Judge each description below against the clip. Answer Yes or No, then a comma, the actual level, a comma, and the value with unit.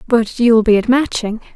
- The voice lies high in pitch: Yes, high, 230 Hz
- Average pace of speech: Yes, average, 195 wpm